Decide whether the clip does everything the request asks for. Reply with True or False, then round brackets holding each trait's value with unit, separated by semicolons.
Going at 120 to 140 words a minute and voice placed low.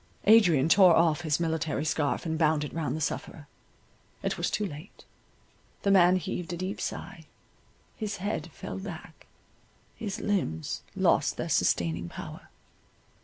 False (135 wpm; 165 Hz)